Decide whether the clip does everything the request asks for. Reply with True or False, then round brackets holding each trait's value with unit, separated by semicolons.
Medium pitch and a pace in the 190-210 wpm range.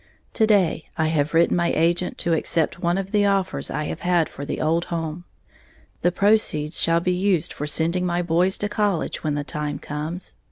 True (170 Hz; 200 wpm)